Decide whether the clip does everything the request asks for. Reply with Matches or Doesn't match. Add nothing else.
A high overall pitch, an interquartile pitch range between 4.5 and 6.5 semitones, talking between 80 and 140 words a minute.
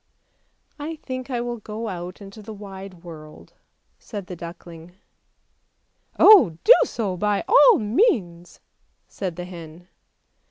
Matches